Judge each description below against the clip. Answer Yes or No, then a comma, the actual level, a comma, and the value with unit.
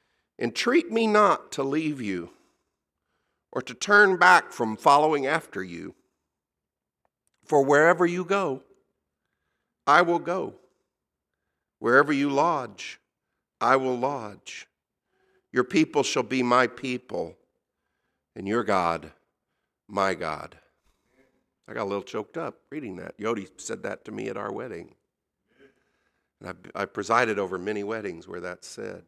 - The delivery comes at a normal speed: No, slow, 130 wpm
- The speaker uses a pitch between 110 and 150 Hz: Yes, low, 135 Hz